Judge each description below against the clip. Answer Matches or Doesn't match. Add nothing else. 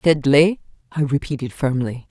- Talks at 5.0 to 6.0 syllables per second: Doesn't match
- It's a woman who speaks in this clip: Matches